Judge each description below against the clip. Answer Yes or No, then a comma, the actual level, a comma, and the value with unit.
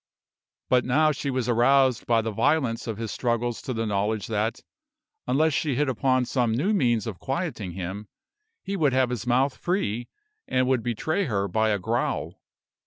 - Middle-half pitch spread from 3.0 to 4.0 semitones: Yes, average, 3.4 semitones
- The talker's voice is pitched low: Yes, low, 120 Hz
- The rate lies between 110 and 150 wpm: No, average, 175 wpm